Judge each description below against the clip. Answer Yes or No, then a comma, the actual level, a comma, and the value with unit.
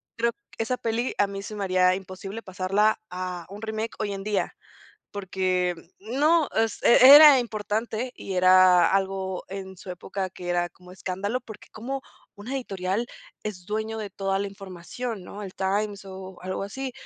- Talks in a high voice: Yes, high, 195 Hz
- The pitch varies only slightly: No, average, 3.0 semitones